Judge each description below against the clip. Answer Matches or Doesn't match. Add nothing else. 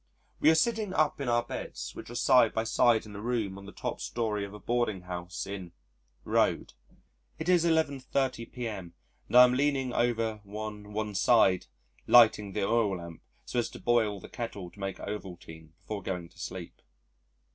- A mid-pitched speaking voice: Doesn't match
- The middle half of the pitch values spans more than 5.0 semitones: Doesn't match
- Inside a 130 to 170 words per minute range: Doesn't match